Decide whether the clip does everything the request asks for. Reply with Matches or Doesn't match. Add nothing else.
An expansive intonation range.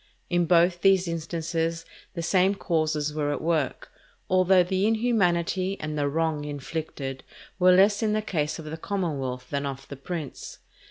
Doesn't match